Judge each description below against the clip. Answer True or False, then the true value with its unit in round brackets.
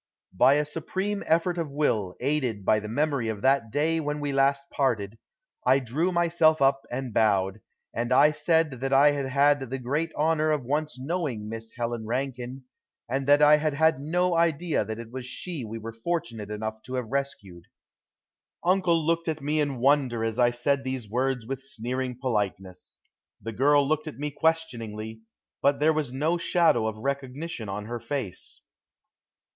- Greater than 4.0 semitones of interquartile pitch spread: True (4.7 semitones)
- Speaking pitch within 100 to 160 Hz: True (135 Hz)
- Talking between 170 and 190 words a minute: True (175 wpm)